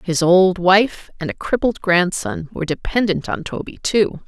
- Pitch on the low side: No, medium, 185 Hz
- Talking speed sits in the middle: Yes, average, 170 wpm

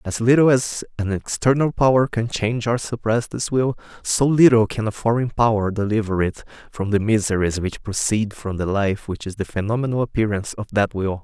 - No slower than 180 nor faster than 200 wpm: Yes, average, 190 wpm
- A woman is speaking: No, male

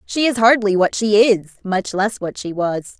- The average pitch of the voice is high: Yes, high, 205 Hz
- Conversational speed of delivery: No, fast, 220 wpm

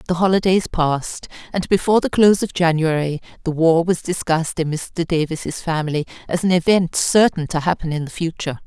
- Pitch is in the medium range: Yes, medium, 170 Hz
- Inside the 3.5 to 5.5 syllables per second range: No, 5.7 syllables/s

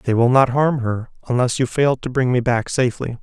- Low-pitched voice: Yes, low, 125 Hz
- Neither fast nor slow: No, fast, 240 wpm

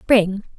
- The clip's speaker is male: No, female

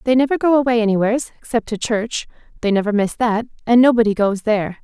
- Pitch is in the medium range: No, high, 225 Hz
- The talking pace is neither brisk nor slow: Yes, average, 175 wpm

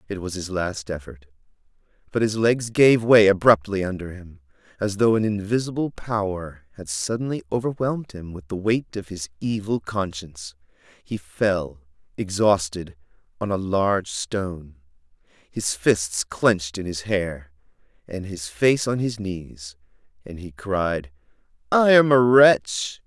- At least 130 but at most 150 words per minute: Yes, average, 140 wpm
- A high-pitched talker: No, very low, 95 Hz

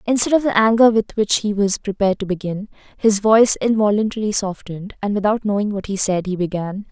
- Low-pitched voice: No, high, 205 Hz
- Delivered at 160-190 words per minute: No, average, 200 wpm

